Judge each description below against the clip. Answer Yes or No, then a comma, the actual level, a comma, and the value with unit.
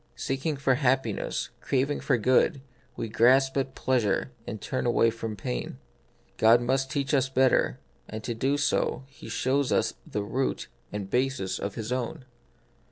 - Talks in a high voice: No, low, 130 Hz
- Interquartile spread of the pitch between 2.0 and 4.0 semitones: Yes, average, 3.1 semitones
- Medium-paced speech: Yes, average, 165 wpm